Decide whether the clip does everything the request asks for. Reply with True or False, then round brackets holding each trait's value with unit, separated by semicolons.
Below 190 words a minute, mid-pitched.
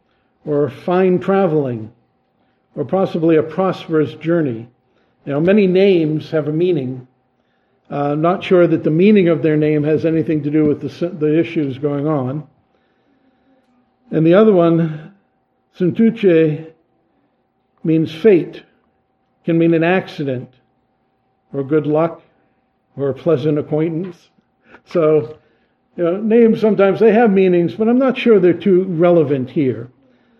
True (135 wpm; 160 Hz)